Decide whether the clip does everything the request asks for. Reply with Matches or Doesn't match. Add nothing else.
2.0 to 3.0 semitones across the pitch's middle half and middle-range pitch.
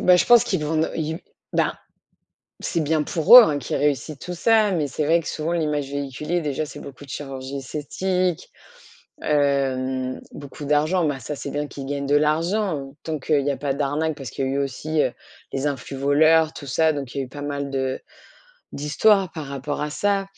Matches